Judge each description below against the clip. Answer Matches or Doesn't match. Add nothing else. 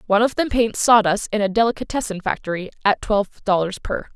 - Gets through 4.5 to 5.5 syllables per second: Doesn't match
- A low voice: Doesn't match